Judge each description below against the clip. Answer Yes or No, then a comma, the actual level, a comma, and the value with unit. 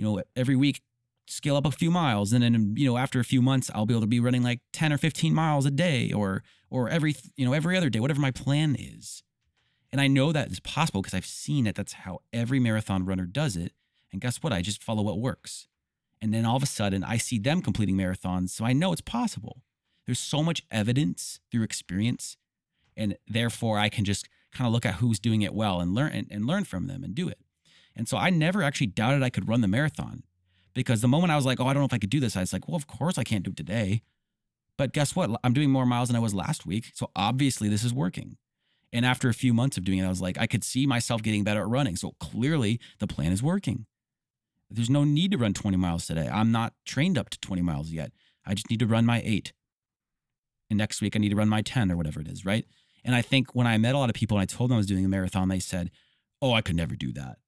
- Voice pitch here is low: Yes, low, 120 Hz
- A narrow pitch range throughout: No, average, 4.7 semitones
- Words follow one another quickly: Yes, fast, 265 wpm